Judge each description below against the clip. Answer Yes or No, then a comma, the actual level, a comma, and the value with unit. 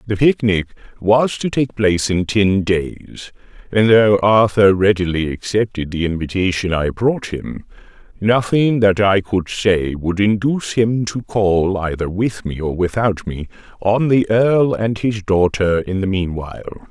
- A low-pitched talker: Yes, low, 100 Hz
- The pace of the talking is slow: No, average, 155 wpm